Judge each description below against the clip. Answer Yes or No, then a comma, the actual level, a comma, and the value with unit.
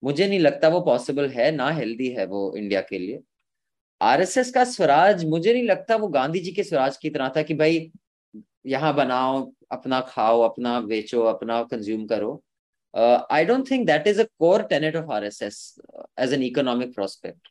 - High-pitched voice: No, medium, 140 Hz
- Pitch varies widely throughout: Yes, wide, 6.6 semitones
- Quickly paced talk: No, average, 180 wpm